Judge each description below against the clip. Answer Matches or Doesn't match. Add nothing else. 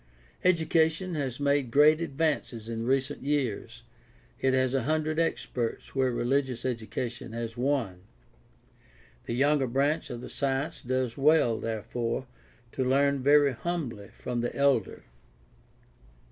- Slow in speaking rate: Matches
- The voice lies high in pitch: Doesn't match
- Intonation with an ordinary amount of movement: Matches